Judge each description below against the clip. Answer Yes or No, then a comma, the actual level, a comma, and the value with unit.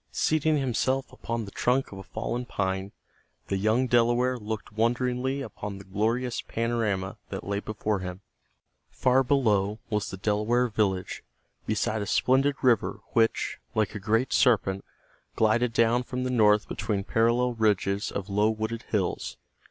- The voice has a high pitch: No, low, 110 Hz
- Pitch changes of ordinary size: Yes, average, 3.2 semitones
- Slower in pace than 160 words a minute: Yes, average, 150 wpm